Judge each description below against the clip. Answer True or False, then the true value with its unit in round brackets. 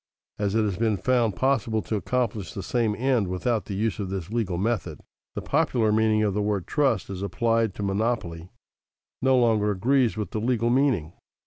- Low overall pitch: True (110 Hz)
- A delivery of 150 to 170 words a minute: False (195 wpm)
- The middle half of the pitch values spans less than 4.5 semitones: True (3.2 semitones)